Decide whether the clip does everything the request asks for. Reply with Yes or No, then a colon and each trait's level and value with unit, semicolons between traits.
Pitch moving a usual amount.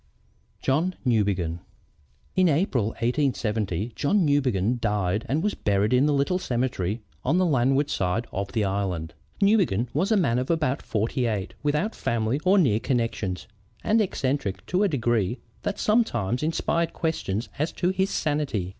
No: wide, 7.4 semitones